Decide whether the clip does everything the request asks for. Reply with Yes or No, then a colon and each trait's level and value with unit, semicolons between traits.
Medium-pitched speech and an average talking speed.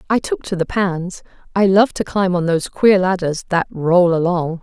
Yes: medium, 180 Hz; average, 195 wpm